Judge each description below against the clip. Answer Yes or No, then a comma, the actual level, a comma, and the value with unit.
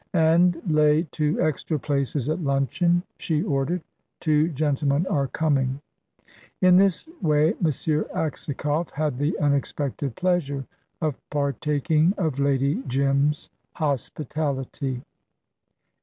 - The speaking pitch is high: No, medium, 150 Hz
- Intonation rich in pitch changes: No, narrow, 2.4 semitones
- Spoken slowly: Yes, slow, 105 wpm